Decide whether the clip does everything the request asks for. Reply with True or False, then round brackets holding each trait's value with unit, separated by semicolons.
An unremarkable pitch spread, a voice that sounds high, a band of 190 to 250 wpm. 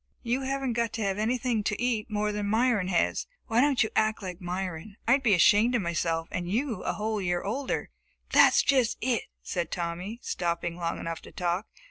True (5.0 semitones; 210 Hz; 200 wpm)